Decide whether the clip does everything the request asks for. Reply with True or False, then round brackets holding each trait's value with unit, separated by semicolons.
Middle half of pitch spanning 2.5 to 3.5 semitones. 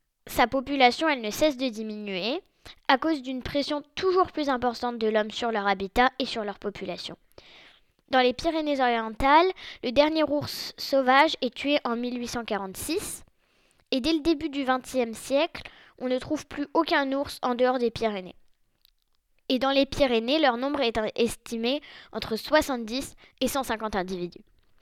False (4.1 semitones)